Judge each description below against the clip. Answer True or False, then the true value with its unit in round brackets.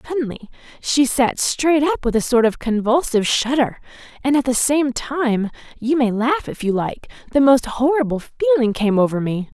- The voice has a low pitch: False (250 Hz)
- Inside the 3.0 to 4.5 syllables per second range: False (4.8 syllables/s)